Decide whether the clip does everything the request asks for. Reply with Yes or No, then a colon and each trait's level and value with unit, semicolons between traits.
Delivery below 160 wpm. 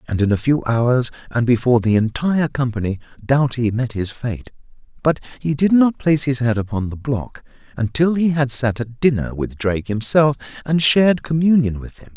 No: average, 190 wpm